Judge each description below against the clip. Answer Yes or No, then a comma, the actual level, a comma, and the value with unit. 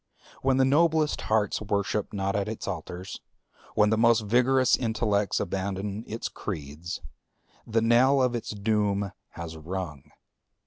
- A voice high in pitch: No, low, 105 Hz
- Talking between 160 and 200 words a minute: No, slow, 135 wpm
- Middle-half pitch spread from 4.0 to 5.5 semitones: No, average, 3.4 semitones